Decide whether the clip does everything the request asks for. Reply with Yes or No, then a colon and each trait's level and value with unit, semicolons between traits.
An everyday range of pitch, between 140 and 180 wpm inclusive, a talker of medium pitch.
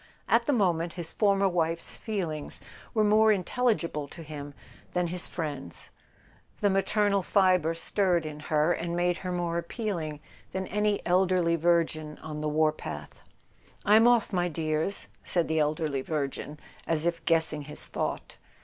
Yes: average, 3.6 semitones; average, 150 wpm; medium, 170 Hz